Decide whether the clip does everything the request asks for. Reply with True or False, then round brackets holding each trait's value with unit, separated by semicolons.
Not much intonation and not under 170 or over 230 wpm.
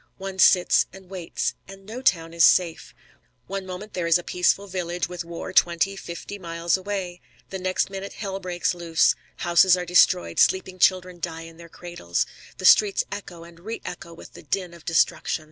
True (2.1 semitones; 180 wpm)